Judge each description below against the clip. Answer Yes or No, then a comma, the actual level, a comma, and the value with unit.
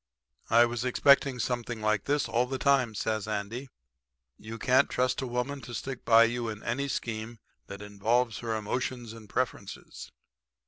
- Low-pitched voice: Yes, low, 120 Hz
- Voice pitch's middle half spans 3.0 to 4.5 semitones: No, narrow, 2.5 semitones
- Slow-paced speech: No, average, 165 wpm